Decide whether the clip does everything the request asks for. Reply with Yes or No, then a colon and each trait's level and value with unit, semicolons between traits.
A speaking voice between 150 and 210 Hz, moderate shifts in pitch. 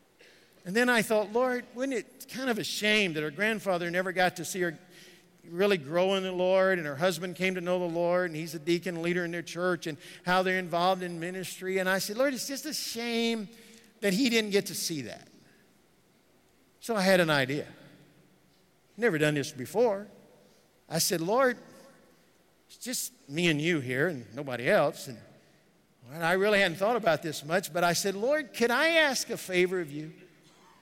Yes: medium, 185 Hz; average, 4.3 semitones